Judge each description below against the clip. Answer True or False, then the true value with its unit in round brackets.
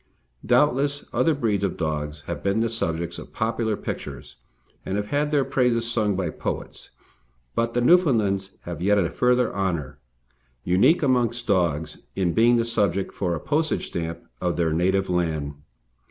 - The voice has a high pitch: False (100 Hz)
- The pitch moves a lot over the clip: True (5.8 semitones)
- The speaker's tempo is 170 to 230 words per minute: False (160 wpm)